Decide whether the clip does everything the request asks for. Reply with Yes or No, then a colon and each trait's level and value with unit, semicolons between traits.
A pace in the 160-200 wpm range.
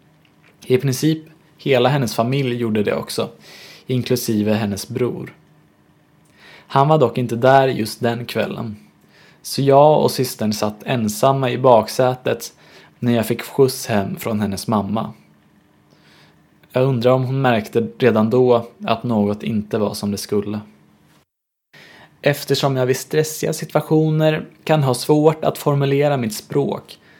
No: average, 135 wpm